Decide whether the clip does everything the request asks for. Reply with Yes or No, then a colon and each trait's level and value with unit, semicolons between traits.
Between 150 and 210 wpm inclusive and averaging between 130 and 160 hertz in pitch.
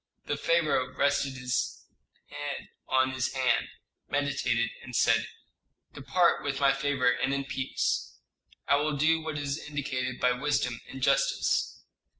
No: average, 140 wpm; low, 135 Hz